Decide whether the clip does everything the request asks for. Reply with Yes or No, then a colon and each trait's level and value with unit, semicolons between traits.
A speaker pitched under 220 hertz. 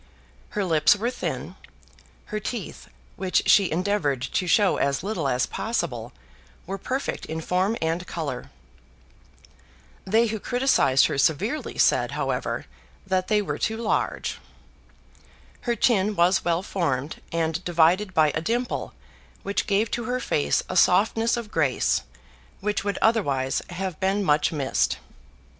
Yes: high, 190 Hz